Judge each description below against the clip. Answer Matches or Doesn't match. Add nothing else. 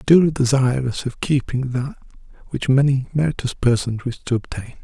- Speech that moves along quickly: Doesn't match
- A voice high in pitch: Doesn't match